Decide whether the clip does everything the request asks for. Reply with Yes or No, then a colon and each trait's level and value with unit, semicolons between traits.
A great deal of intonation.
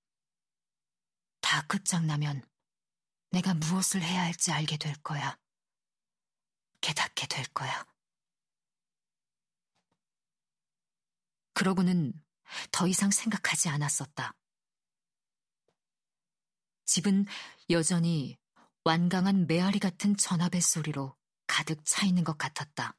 No: average, 3.0 semitones